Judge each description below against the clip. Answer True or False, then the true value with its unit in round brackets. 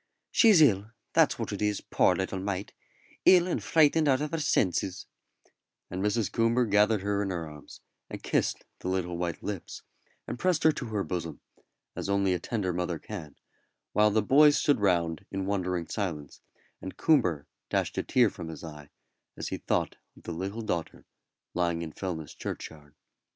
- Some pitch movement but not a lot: True (4.7 semitones)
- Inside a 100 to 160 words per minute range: False (175 wpm)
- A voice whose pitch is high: False (95 Hz)